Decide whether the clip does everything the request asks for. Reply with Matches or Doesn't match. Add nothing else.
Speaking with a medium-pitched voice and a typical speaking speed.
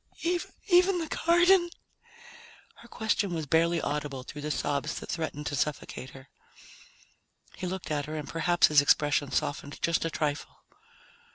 Matches